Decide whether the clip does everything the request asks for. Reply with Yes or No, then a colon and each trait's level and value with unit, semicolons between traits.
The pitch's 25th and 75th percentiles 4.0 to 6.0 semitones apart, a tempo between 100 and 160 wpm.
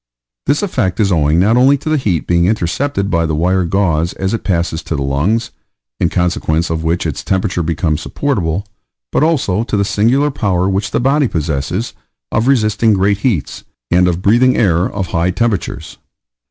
No: average, 5.2 semitones; average, 180 wpm